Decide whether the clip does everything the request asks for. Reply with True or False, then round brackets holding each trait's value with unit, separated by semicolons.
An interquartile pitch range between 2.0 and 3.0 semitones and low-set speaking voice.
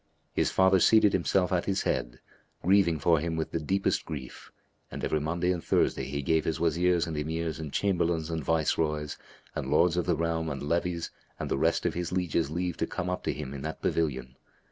True (2.4 semitones; 80 Hz)